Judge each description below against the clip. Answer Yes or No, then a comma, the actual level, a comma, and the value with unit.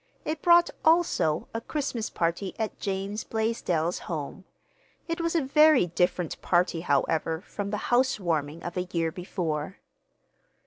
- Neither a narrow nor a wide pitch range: No, wide, 6.8 semitones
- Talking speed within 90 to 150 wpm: Yes, slow, 135 wpm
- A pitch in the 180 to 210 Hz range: Yes, high, 190 Hz